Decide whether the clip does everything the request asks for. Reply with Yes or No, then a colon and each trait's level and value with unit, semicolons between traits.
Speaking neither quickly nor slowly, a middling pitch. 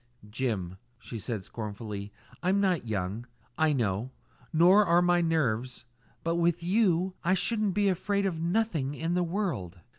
Yes: average, 150 wpm; medium, 165 Hz